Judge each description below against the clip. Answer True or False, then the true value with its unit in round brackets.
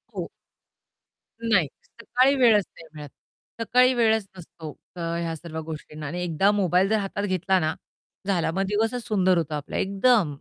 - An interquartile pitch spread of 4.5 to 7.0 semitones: True (5.2 semitones)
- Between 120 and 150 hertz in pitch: False (190 Hz)